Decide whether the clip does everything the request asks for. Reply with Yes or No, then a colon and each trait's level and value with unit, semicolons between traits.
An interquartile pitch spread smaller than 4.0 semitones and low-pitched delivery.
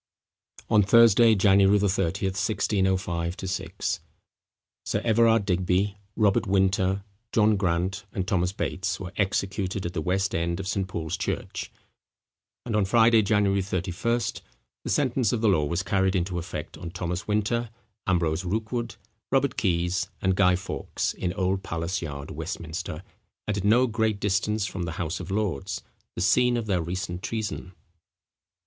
Yes: average, 2.8 semitones; very low, 95 Hz